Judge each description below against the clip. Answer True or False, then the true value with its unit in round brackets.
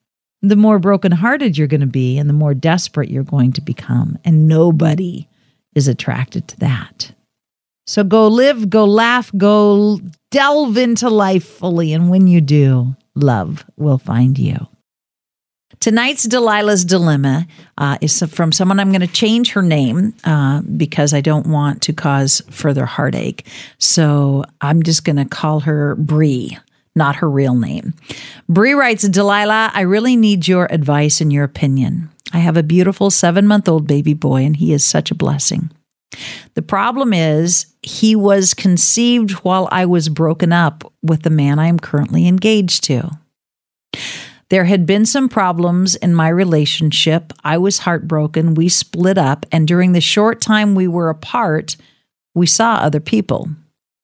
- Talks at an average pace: True (160 wpm)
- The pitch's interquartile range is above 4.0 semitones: True (5.0 semitones)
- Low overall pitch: False (165 Hz)